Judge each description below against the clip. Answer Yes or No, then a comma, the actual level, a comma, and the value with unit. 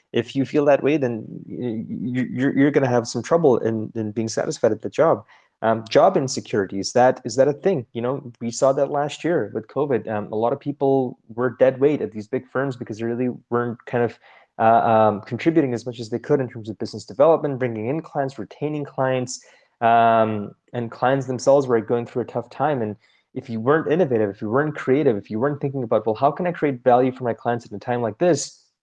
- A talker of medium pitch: No, low, 125 Hz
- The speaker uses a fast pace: Yes, fast, 225 wpm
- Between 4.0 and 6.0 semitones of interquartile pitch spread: No, average, 3.3 semitones